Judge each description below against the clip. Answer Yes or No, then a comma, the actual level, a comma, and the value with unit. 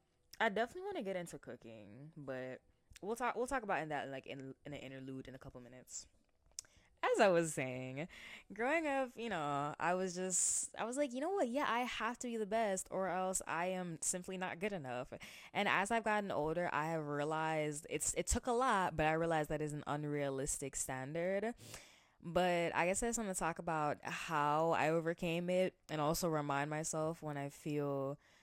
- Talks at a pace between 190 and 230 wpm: Yes, fast, 205 wpm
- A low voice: No, medium, 165 Hz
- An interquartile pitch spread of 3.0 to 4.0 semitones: No, wide, 5.6 semitones